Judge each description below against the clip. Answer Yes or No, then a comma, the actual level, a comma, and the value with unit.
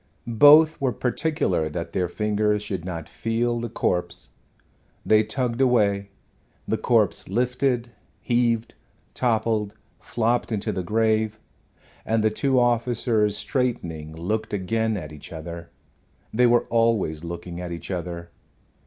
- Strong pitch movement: No, average, 5.0 semitones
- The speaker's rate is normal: No, slow, 125 wpm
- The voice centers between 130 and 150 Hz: No, low, 110 Hz